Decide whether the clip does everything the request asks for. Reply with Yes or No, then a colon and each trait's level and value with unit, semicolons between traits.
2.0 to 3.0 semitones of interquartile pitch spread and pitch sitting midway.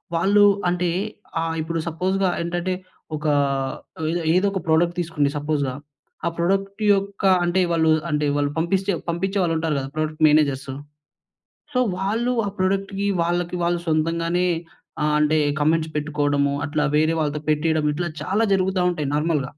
No: average, 3.6 semitones; medium, 165 Hz